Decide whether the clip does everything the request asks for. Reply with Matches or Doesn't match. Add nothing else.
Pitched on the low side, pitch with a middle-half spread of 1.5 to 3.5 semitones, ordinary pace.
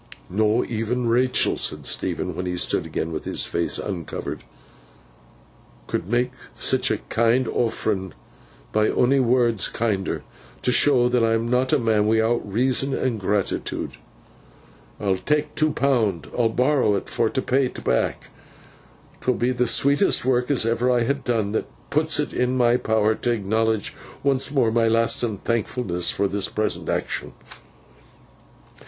Matches